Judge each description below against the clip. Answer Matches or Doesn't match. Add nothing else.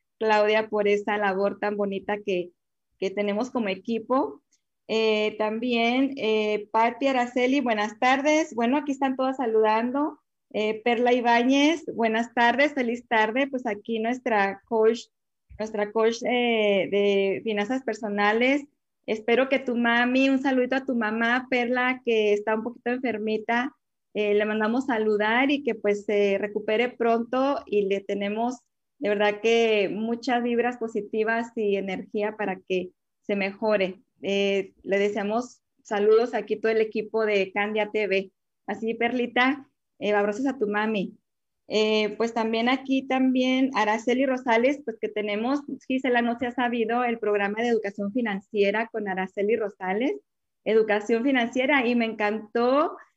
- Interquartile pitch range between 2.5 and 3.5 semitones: Matches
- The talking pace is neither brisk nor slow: Matches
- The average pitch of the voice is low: Doesn't match